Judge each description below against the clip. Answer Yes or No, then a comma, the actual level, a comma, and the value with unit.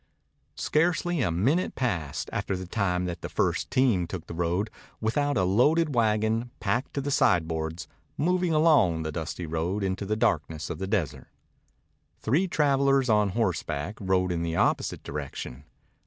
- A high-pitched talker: No, low, 100 Hz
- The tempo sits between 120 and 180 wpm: Yes, average, 155 wpm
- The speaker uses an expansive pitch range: Yes, wide, 7.7 semitones